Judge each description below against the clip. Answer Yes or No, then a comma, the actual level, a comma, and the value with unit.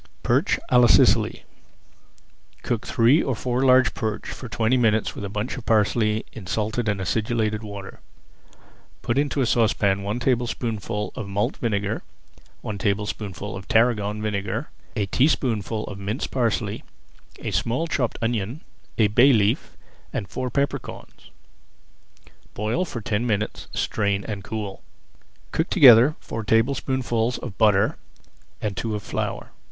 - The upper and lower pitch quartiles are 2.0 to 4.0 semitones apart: Yes, average, 2.9 semitones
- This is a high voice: No, low, 110 Hz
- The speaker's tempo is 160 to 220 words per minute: No, average, 140 wpm